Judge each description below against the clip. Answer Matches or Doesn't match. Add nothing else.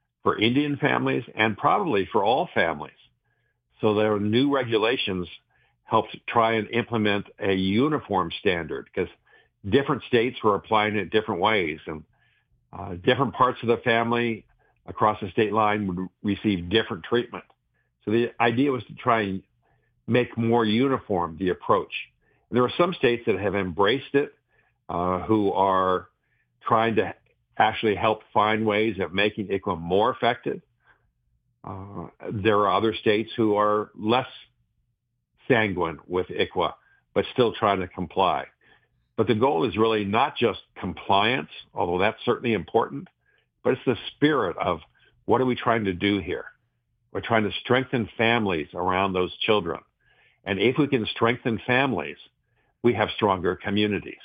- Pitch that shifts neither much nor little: Matches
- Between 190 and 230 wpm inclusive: Doesn't match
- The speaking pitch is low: Matches